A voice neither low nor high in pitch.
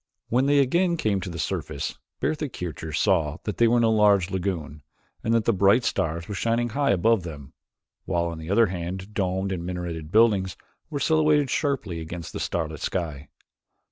No: very low, 95 Hz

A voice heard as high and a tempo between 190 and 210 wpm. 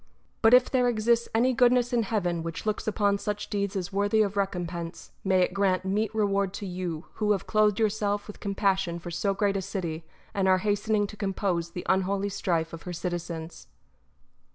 Yes: high, 200 Hz; average, 195 wpm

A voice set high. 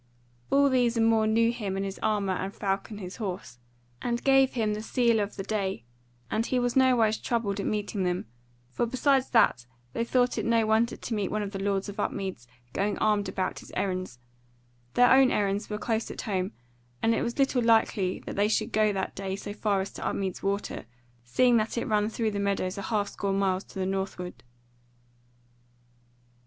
Yes: high, 210 Hz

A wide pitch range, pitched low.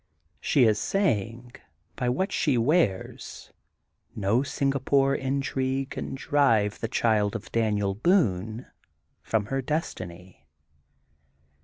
No: average, 4.8 semitones; low, 120 Hz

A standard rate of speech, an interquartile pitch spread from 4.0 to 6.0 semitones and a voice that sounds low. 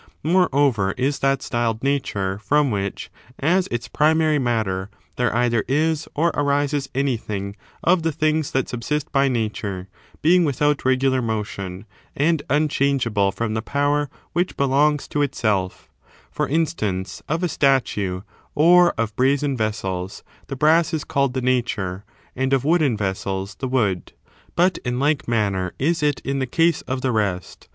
Yes: average, 155 wpm; wide, 5.4 semitones; low, 130 Hz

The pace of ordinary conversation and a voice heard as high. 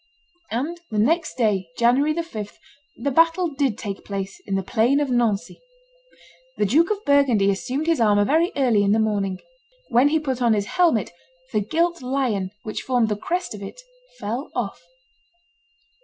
Yes: average, 170 wpm; high, 245 Hz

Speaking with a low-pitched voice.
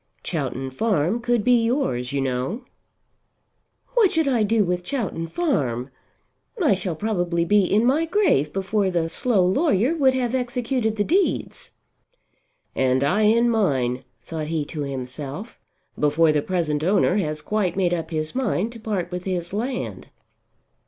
No: high, 190 Hz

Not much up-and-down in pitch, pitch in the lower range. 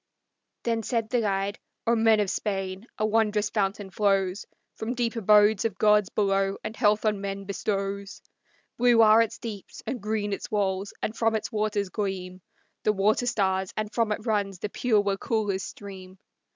No: narrow, 2.0 semitones; high, 210 Hz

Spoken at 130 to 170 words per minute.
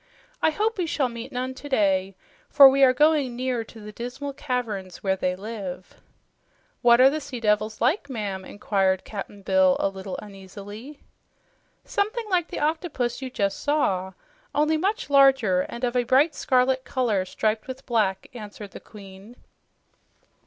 Yes: average, 160 wpm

